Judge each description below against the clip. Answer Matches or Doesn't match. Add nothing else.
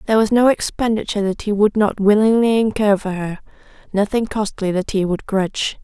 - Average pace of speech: Matches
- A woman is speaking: Matches